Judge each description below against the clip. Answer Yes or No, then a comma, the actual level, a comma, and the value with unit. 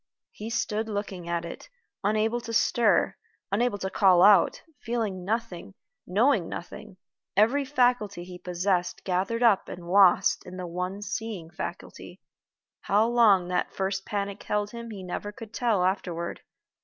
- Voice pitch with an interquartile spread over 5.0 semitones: No, average, 3.6 semitones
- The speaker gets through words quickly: No, average, 145 wpm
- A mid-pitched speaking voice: No, high, 200 Hz